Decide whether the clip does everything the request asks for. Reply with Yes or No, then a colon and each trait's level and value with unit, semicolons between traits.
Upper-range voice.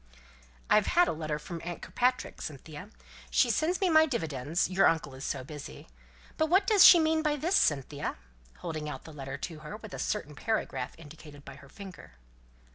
No: medium, 165 Hz